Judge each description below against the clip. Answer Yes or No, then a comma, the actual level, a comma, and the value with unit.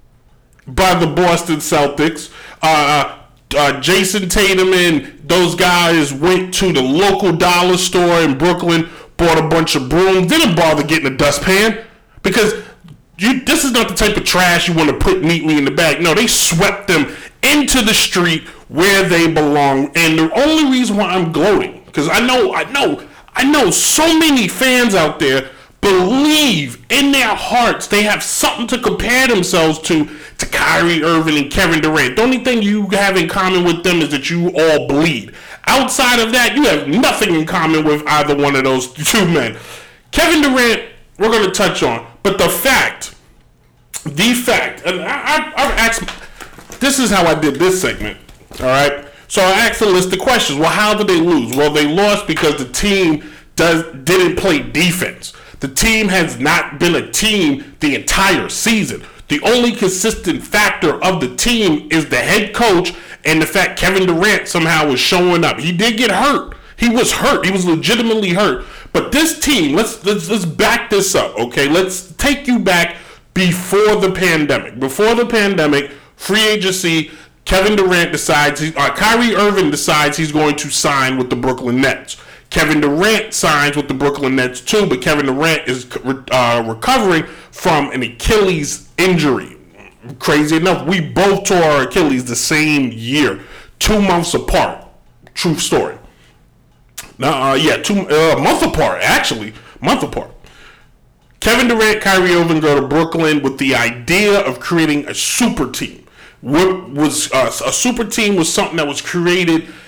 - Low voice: No, medium, 175 Hz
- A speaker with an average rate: Yes, average, 170 wpm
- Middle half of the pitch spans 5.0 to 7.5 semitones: Yes, wide, 5.6 semitones